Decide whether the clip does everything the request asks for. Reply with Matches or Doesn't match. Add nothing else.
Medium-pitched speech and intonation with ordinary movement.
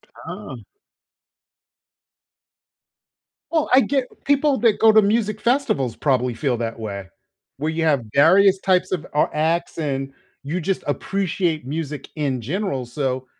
Doesn't match